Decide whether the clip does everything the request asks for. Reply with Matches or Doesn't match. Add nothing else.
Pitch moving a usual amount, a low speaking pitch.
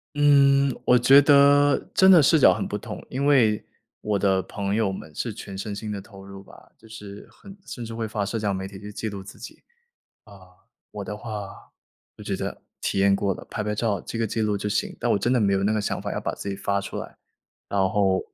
Matches